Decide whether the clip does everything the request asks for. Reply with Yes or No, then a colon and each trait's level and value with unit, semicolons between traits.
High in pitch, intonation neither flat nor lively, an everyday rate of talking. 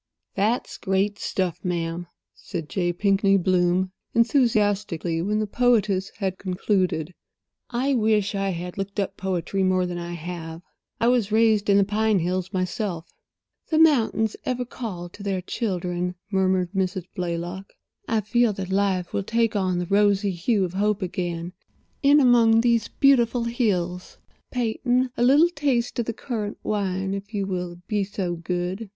Yes: high, 195 Hz; average, 3.7 semitones; average, 155 wpm